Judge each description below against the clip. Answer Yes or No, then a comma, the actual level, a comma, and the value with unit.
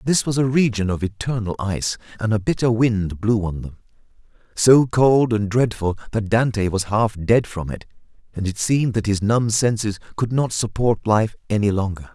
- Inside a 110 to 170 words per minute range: No, average, 190 wpm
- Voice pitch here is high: No, low, 110 Hz